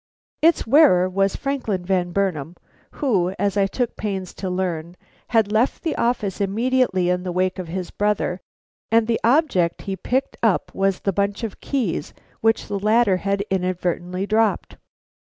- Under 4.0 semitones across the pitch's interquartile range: Yes, average, 3.5 semitones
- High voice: Yes, high, 195 Hz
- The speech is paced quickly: No, average, 160 wpm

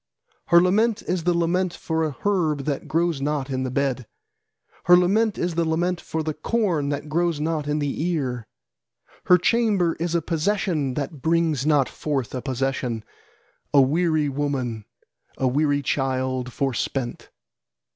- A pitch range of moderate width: Yes, average, 4.2 semitones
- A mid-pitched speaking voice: Yes, medium, 150 Hz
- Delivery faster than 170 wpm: No, average, 155 wpm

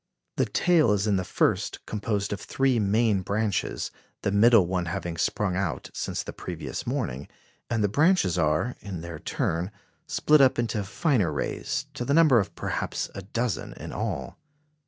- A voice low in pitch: Yes, low, 105 Hz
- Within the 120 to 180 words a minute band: Yes, average, 170 wpm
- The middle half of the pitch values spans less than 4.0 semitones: No, average, 4.7 semitones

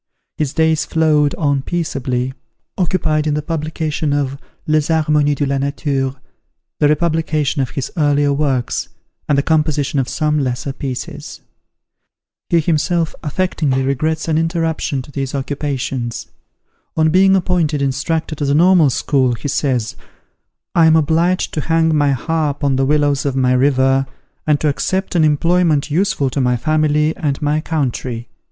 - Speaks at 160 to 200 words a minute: No, average, 150 wpm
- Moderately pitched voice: Yes, medium, 150 Hz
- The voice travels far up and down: No, average, 2.7 semitones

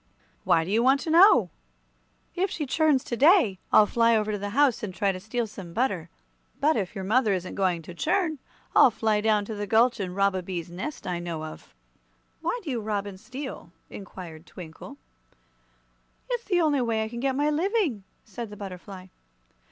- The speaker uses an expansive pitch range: Yes, wide, 6.2 semitones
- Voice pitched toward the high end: Yes, high, 215 Hz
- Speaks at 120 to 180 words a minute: No, average, 200 wpm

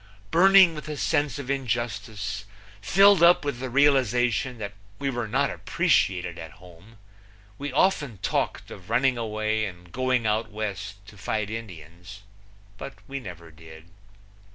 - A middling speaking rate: Yes, average, 145 wpm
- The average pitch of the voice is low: Yes, low, 110 Hz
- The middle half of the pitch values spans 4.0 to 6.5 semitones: Yes, average, 5.2 semitones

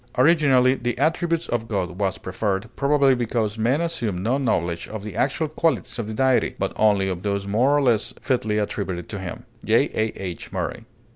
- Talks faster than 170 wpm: Yes, average, 190 wpm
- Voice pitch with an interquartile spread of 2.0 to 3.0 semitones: No, average, 5.2 semitones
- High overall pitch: No, low, 115 Hz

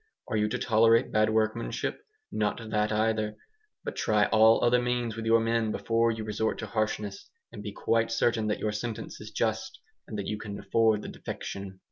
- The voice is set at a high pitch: No, low, 110 Hz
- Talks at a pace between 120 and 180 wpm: No, average, 190 wpm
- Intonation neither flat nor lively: No, narrow, 1.2 semitones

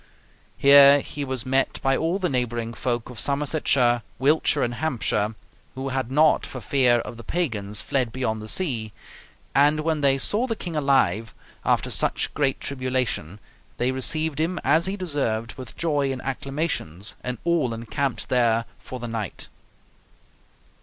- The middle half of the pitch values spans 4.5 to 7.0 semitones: No, average, 4.0 semitones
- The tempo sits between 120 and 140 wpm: No, average, 155 wpm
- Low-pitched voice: Yes, low, 130 Hz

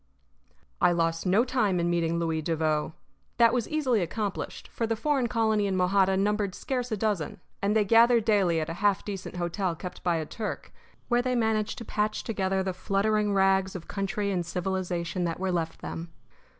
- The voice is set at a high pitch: Yes, high, 195 Hz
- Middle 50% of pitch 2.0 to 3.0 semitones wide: No, average, 3.9 semitones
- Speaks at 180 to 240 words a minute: Yes, average, 190 wpm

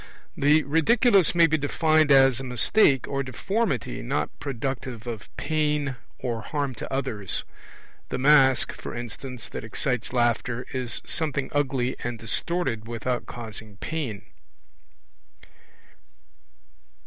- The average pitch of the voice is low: Yes, low, 130 Hz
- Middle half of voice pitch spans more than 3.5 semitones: Yes, average, 3.9 semitones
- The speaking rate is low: Yes, slow, 115 wpm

